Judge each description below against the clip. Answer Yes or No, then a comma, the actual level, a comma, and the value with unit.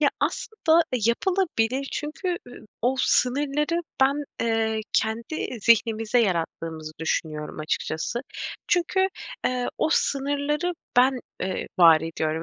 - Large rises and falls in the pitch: Yes, wide, 7.6 semitones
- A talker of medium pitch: No, high, 245 Hz